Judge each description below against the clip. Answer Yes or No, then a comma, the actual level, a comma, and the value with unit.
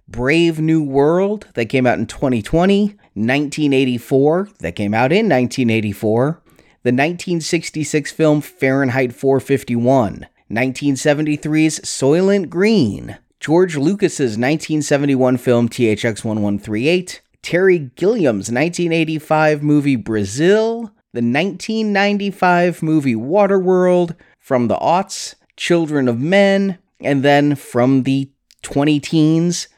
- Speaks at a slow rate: Yes, slow, 100 wpm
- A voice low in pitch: No, medium, 150 Hz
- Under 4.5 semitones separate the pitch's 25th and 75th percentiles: No, average, 5.2 semitones